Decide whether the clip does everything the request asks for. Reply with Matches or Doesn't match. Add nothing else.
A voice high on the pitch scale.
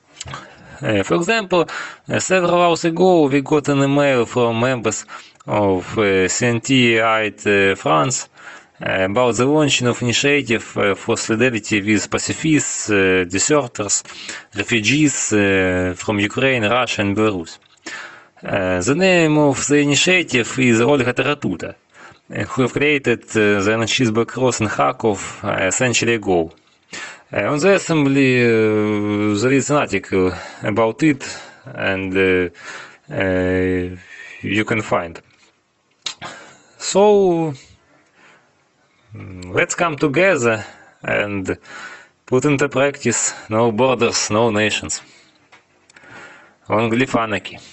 Doesn't match